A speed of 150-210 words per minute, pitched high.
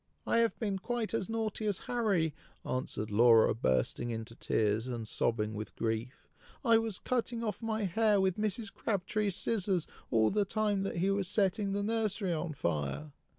Yes: average, 170 wpm; high, 195 Hz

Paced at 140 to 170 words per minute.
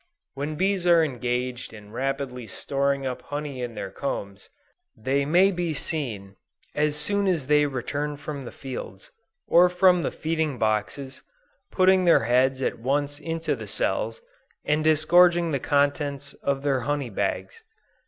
Yes: average, 150 wpm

